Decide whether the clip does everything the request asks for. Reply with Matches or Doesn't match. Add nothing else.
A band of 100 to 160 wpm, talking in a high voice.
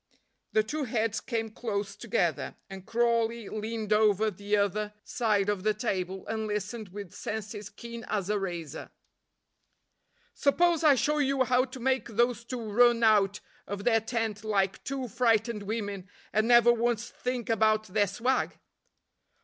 Matches